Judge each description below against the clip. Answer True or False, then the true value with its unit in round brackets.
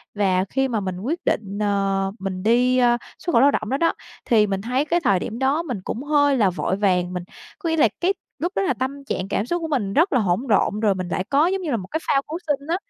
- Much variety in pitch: True (6.8 semitones)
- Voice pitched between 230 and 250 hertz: True (240 Hz)